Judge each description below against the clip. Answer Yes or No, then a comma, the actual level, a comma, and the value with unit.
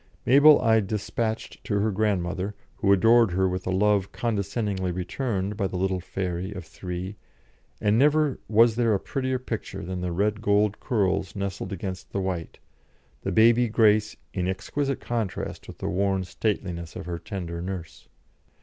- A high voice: No, low, 100 Hz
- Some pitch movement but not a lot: Yes, average, 3.2 semitones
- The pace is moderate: Yes, average, 160 wpm